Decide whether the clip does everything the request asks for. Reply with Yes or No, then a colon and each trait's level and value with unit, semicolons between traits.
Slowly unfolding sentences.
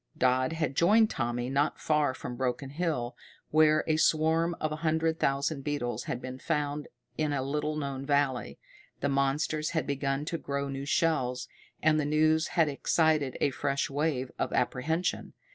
No: average, 165 wpm